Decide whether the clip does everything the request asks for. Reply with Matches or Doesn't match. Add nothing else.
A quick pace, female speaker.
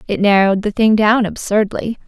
Doesn't match